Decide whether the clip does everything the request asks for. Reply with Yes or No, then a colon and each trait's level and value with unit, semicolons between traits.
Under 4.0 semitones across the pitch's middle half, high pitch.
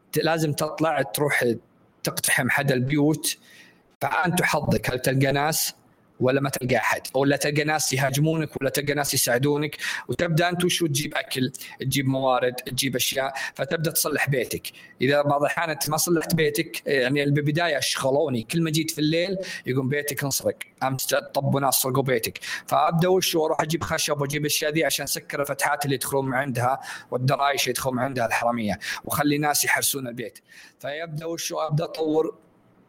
No: average, 2.9 semitones; medium, 145 Hz